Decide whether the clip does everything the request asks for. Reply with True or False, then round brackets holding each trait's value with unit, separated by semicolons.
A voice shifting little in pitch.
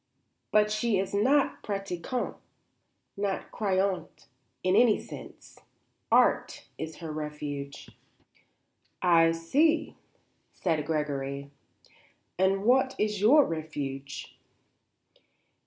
False (5.6 semitones)